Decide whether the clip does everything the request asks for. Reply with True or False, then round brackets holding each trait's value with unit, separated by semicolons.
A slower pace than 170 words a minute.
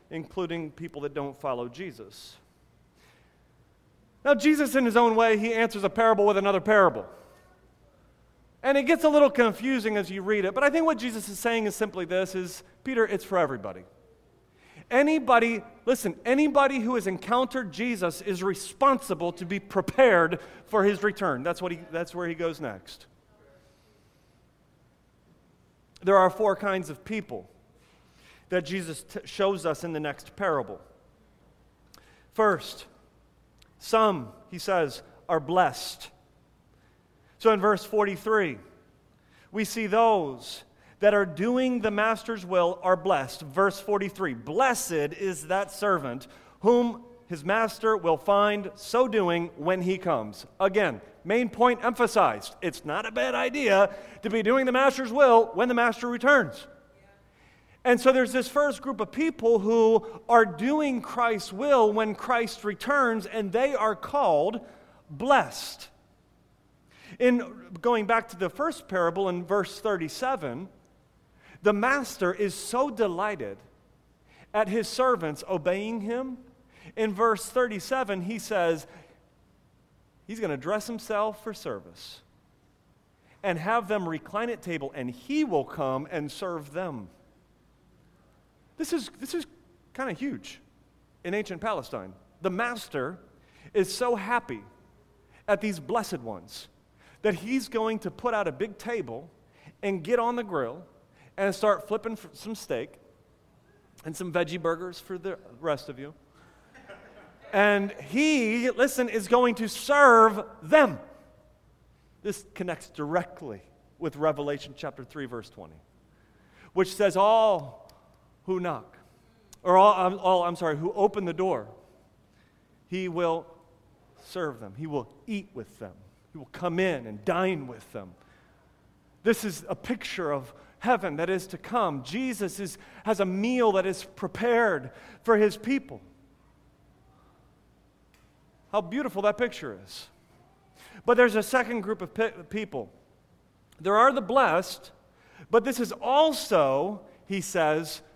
True (140 wpm)